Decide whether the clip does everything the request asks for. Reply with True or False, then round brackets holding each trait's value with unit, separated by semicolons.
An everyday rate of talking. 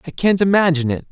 False (215 wpm)